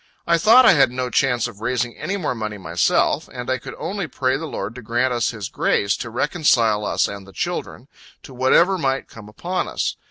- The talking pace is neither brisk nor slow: No, fast, 215 wpm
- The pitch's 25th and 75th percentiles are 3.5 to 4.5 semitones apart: No, average, 5.0 semitones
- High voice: No, low, 125 Hz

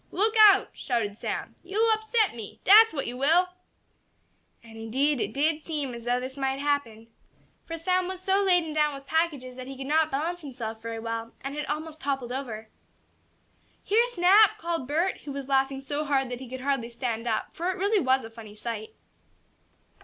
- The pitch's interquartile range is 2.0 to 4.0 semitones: No, wide, 5.5 semitones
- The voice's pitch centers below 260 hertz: No, very high, 275 Hz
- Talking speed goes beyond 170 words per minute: Yes, average, 190 wpm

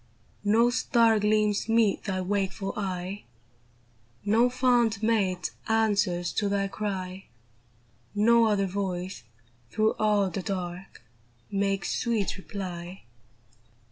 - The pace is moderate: No, slow, 105 wpm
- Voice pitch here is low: No, high, 200 Hz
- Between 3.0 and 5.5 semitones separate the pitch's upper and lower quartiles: No, narrow, 2.6 semitones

